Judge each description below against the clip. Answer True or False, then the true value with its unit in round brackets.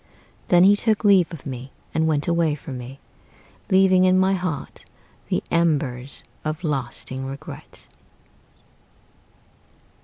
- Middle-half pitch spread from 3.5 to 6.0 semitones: True (5.3 semitones)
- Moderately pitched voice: True (160 Hz)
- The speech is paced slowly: True (120 wpm)